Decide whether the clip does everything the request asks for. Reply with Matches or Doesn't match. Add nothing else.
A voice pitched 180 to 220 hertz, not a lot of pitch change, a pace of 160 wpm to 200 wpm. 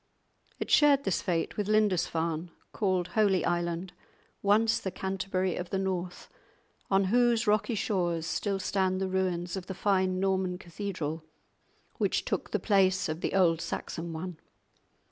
Doesn't match